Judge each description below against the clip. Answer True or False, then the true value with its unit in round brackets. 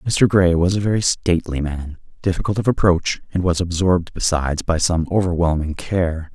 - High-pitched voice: False (90 Hz)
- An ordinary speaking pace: True (170 wpm)